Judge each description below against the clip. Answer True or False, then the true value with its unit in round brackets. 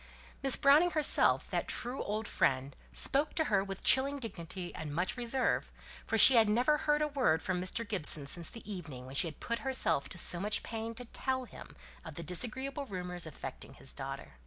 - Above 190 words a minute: True (200 wpm)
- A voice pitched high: True (210 Hz)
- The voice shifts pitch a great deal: True (7.9 semitones)